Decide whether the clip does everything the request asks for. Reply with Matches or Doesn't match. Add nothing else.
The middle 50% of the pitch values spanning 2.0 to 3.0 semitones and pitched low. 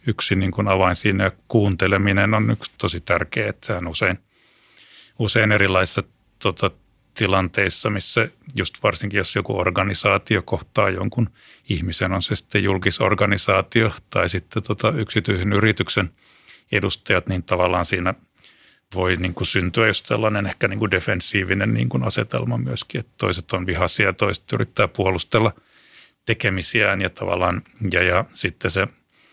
Matches